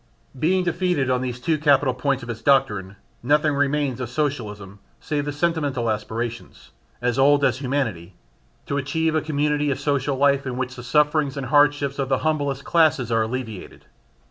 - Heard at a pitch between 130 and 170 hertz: Yes, medium, 140 Hz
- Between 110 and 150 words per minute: No, average, 170 wpm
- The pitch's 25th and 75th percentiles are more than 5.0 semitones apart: No, average, 3.0 semitones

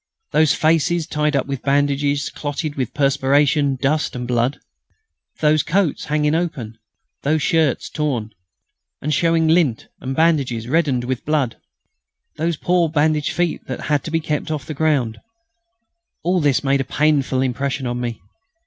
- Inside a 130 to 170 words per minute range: Yes, average, 150 wpm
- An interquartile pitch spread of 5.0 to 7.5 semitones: No, average, 3.0 semitones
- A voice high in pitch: No, medium, 145 Hz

